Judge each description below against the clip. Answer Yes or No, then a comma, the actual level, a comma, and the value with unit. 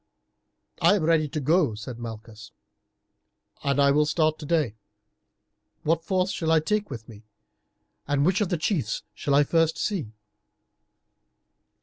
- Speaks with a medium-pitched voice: Yes, medium, 155 Hz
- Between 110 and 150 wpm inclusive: Yes, slow, 135 wpm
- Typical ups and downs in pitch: Yes, average, 3.4 semitones